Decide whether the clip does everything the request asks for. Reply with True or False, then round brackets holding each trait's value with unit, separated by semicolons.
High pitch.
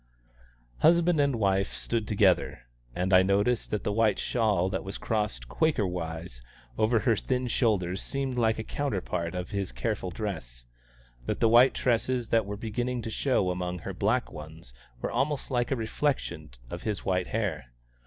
False (105 Hz)